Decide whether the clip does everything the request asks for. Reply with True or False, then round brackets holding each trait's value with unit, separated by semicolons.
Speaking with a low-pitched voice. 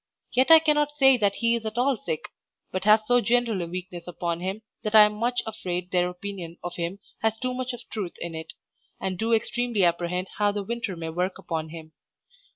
False (200 Hz)